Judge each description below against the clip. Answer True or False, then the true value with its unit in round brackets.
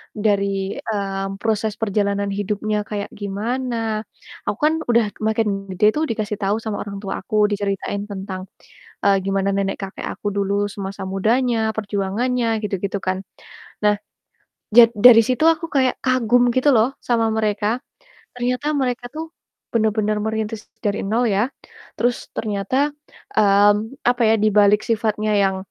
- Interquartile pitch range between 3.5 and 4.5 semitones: False (2.7 semitones)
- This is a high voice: True (210 Hz)